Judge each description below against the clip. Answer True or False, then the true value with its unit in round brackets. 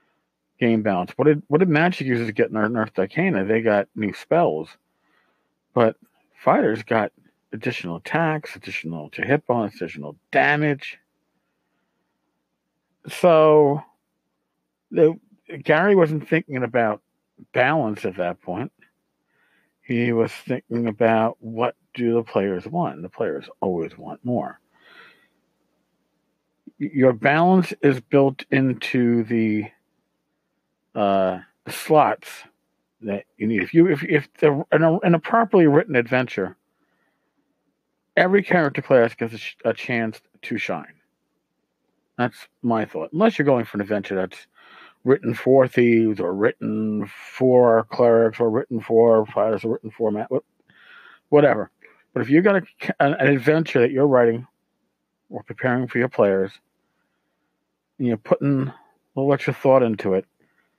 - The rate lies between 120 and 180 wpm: True (135 wpm)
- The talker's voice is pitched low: True (120 Hz)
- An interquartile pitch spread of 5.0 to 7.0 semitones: True (5.3 semitones)